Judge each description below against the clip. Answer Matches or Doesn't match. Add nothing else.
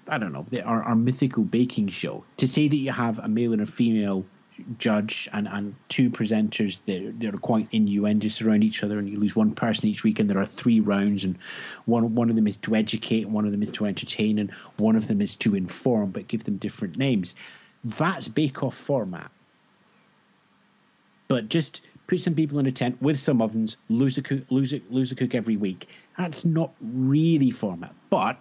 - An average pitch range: Matches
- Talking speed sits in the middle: Doesn't match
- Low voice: Matches